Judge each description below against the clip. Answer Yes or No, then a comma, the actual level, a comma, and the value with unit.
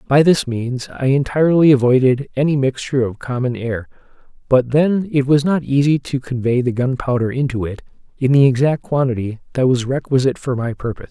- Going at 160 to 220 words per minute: Yes, average, 180 wpm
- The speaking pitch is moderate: No, low, 130 Hz